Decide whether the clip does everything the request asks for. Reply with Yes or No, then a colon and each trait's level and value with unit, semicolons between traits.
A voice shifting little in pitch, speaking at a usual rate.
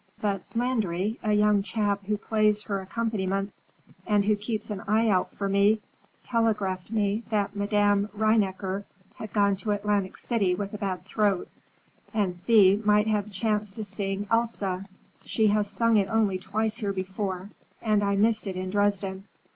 Yes: narrow, 1.5 semitones; average, 165 wpm